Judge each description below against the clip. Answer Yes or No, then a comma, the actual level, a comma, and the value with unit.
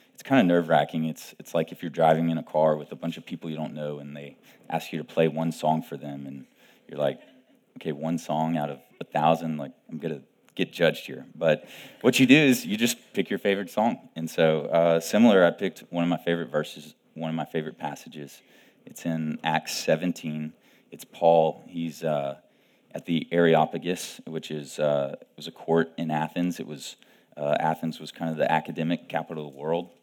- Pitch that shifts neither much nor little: No, narrow, 1.4 semitones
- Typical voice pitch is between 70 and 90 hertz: Yes, very low, 80 Hz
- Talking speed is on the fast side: Yes, fast, 220 wpm